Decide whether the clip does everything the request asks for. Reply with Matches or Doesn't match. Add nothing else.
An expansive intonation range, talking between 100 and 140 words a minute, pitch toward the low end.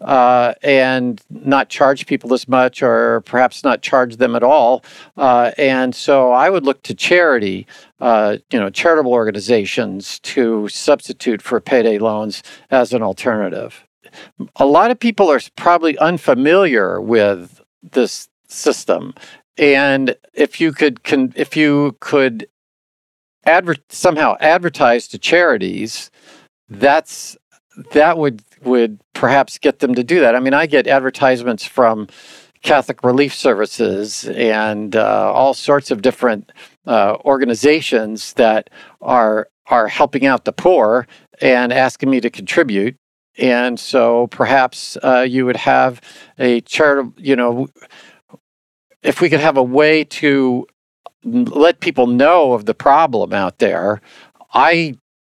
Doesn't match